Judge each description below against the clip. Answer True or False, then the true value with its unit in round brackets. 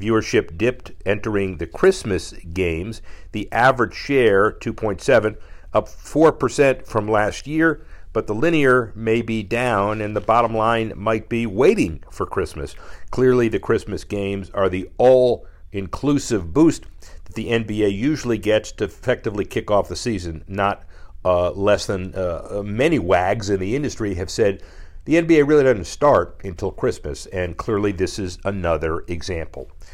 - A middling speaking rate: True (150 wpm)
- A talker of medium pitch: False (105 Hz)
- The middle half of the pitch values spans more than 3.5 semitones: True (3.9 semitones)